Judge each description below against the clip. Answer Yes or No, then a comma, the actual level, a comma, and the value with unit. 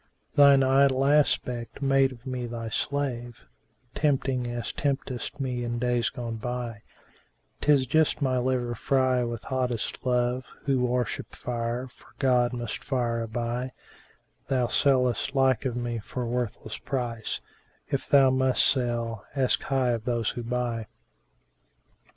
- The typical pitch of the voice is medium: No, low, 125 Hz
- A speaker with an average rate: Yes, average, 145 wpm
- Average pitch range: No, narrow, 1.9 semitones